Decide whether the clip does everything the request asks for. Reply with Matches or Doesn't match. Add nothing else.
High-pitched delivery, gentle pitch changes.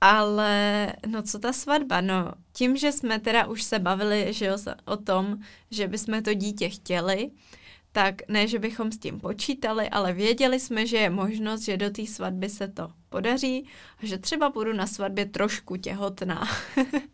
Matches